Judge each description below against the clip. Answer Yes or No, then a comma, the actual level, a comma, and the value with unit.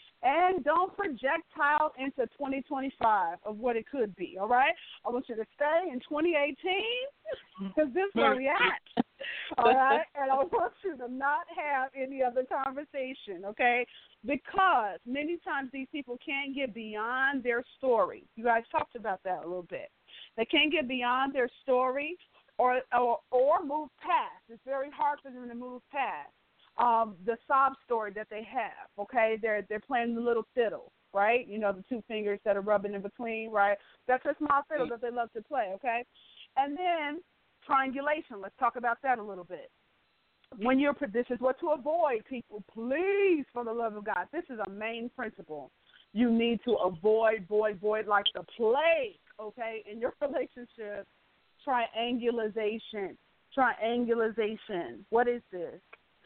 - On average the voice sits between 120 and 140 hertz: No, high, 245 Hz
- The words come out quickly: No, average, 165 wpm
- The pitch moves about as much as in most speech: Yes, average, 4.5 semitones